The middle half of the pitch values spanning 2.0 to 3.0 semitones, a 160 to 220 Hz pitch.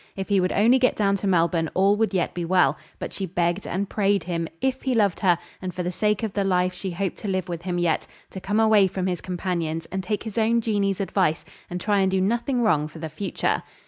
Yes: average, 2.7 semitones; high, 190 Hz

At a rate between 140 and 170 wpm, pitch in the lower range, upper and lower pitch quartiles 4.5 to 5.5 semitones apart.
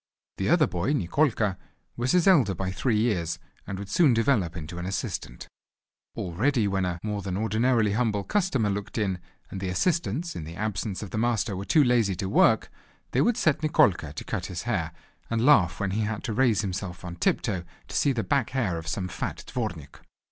No: average, 200 wpm; low, 105 Hz; average, 5.0 semitones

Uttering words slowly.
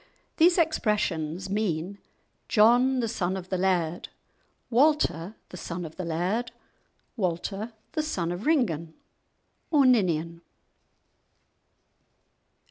Yes: slow, 105 wpm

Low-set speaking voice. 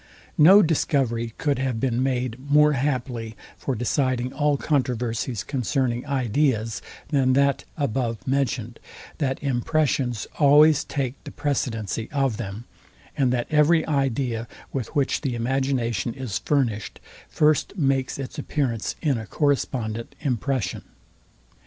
Yes: low, 130 Hz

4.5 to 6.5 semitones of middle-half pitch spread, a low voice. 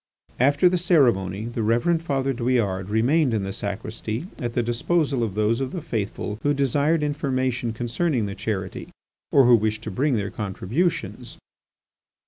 Yes: average, 4.8 semitones; low, 120 Hz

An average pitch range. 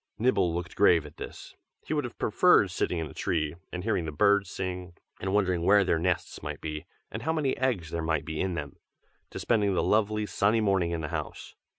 Yes: average, 4.0 semitones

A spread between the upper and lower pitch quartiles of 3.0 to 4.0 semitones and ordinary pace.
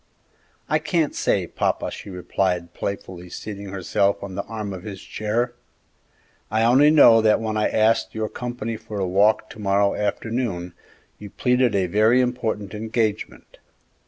No: narrow, 2.5 semitones; average, 155 wpm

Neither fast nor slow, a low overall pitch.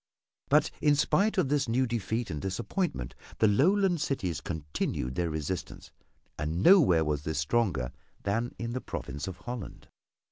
Yes: average, 150 wpm; low, 105 Hz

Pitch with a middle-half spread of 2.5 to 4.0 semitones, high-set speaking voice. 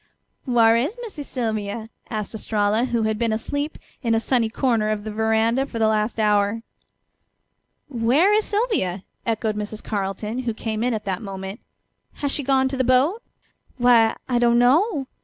Yes: average, 3.3 semitones; high, 230 Hz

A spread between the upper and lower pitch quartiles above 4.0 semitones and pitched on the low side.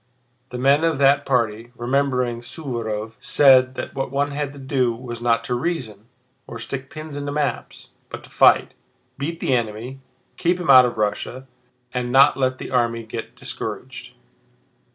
No: average, 3.0 semitones; low, 130 Hz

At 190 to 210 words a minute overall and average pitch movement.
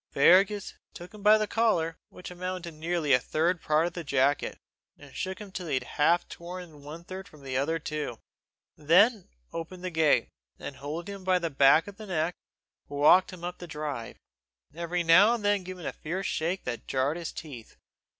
Yes: average, 200 wpm; average, 3.5 semitones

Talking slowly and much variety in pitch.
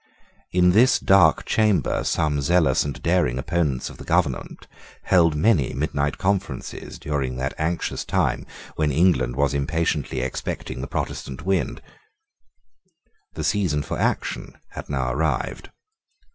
No: slow, 130 wpm; average, 4.6 semitones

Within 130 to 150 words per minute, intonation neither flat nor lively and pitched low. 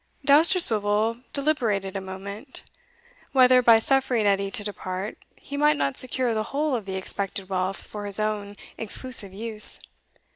No: average, 145 wpm; average, 4.5 semitones; high, 215 Hz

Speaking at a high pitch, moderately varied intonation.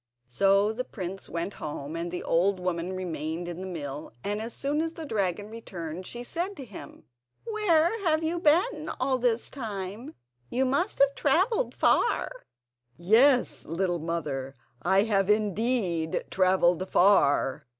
No: high, 195 Hz; wide, 7.5 semitones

